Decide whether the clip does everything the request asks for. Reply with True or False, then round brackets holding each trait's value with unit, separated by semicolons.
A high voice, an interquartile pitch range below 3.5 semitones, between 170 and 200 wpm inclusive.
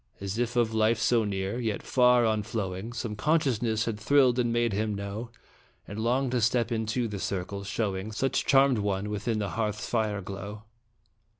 False (110 Hz; 2.7 semitones; 180 wpm)